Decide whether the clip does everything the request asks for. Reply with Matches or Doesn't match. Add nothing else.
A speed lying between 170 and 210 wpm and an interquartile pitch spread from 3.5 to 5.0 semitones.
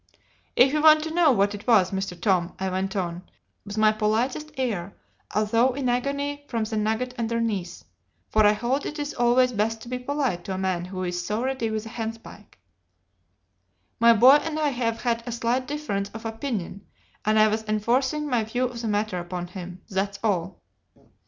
Matches